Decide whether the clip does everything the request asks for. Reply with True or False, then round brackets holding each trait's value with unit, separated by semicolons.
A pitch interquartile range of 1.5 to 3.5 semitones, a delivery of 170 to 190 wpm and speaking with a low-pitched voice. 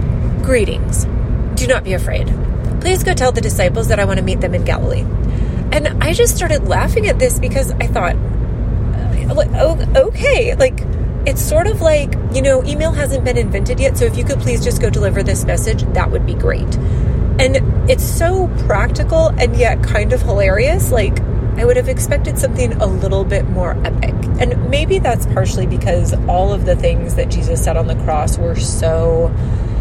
True (3.2 semitones; 185 wpm; 110 Hz)